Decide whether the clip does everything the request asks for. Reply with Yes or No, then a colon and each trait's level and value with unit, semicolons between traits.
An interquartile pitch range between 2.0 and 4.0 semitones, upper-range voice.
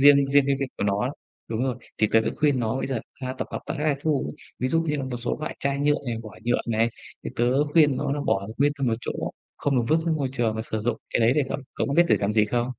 No: average, 3.7 semitones; low, 130 Hz